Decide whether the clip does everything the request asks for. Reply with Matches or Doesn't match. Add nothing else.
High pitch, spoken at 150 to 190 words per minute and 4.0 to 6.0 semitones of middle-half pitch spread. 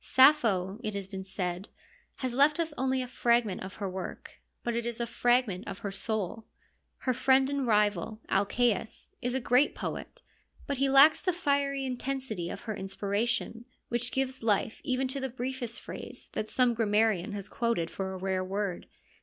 Matches